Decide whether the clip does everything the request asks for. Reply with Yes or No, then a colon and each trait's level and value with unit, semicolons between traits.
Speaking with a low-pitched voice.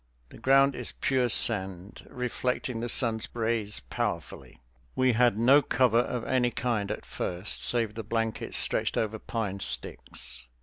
Yes: low, 115 Hz